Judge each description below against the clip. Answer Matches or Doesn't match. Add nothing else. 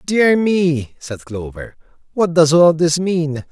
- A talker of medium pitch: Matches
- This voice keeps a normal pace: Matches